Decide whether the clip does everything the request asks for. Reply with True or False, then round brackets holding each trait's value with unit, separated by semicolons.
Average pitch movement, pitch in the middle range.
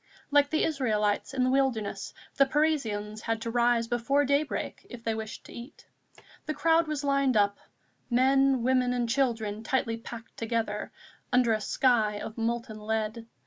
False (3.6 semitones; 240 Hz)